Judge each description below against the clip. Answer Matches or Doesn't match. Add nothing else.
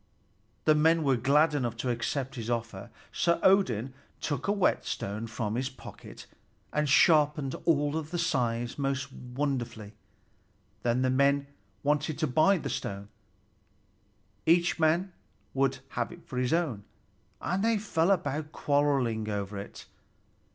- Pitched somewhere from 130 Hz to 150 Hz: Matches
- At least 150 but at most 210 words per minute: Doesn't match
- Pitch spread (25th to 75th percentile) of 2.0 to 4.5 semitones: Doesn't match